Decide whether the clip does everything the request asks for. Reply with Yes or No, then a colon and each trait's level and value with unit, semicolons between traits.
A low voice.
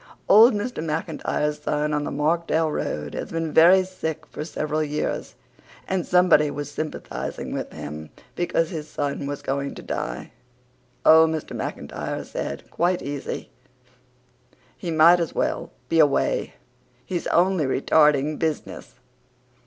No: medium, 155 Hz